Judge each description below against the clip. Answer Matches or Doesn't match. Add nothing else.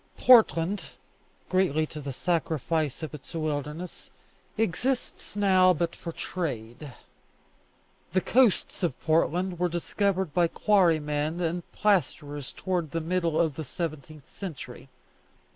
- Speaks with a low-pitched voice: Doesn't match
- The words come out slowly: Matches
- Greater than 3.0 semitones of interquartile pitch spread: Matches